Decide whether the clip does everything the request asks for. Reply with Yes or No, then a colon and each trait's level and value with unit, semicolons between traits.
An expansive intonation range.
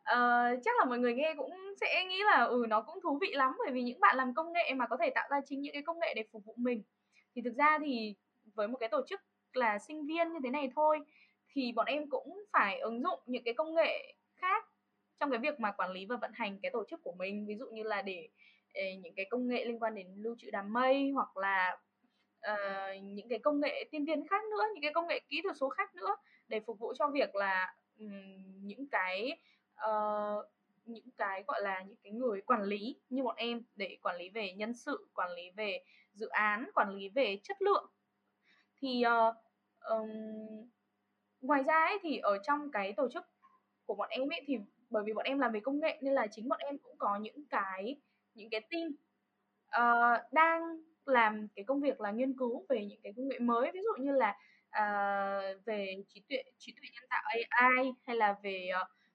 Yes: wide, 5.7 semitones